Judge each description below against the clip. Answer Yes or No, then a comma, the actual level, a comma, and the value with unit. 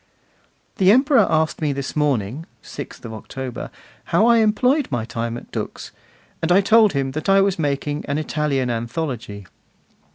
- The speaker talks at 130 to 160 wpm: Yes, average, 155 wpm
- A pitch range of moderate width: No, wide, 7.3 semitones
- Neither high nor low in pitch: Yes, medium, 150 Hz